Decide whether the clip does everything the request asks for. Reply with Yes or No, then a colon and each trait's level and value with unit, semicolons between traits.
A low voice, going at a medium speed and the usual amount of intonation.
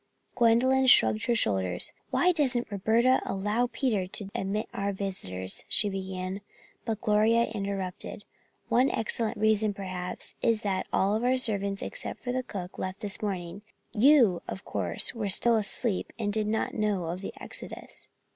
No: high, 210 Hz; average, 150 wpm; average, 3.4 semitones